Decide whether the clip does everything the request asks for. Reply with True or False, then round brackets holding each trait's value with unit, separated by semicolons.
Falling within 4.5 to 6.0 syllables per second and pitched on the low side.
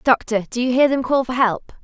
False (5.3 syllables/s; 245 Hz)